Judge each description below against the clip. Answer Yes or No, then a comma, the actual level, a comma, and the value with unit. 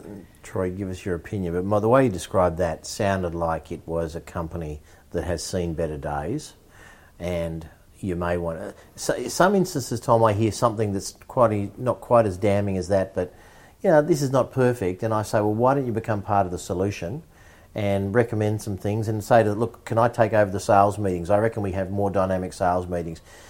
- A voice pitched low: Yes, low, 100 Hz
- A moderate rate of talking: No, fast, 220 wpm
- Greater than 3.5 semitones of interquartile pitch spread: Yes, average, 4.0 semitones